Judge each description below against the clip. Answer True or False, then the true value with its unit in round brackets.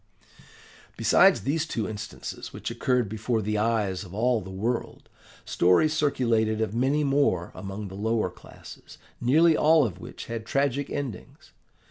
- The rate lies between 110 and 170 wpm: True (145 wpm)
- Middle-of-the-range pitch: False (115 Hz)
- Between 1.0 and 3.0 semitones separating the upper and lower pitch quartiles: False (4.9 semitones)